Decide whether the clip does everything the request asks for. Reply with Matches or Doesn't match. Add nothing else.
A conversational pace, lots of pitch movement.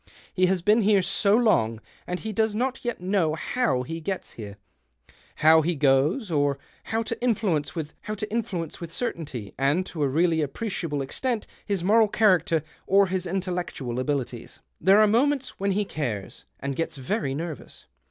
Matches